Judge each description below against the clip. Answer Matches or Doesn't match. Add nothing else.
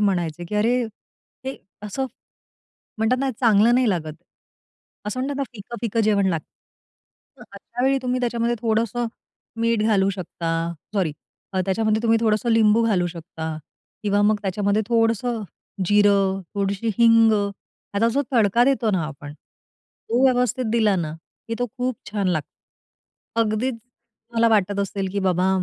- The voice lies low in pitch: Doesn't match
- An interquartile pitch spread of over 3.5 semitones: Doesn't match